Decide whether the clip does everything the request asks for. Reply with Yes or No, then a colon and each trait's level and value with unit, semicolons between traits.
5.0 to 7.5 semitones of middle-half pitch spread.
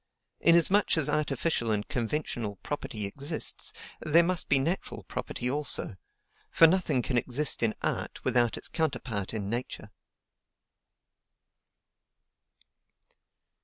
Yes: average, 5.3 semitones